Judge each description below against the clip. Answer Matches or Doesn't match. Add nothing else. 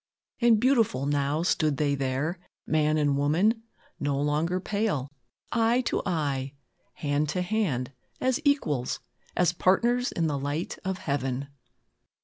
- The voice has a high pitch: Doesn't match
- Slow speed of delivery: Matches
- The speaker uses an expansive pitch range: Matches